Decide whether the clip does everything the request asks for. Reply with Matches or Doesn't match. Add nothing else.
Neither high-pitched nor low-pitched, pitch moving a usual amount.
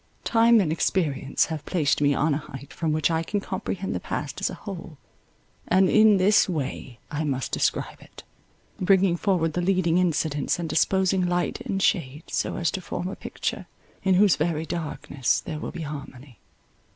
Matches